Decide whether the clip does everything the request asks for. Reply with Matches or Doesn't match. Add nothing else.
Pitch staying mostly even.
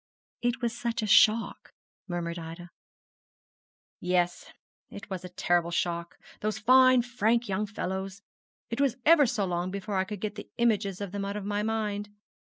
Doesn't match